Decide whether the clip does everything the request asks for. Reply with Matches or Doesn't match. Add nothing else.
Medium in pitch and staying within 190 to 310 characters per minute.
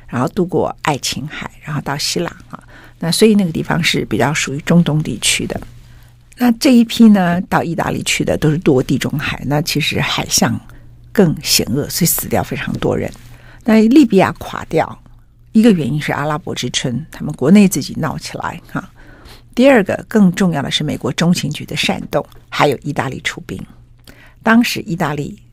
Matches